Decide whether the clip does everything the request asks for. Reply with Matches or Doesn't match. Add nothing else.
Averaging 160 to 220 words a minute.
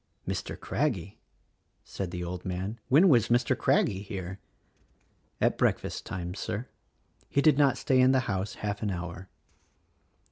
Doesn't match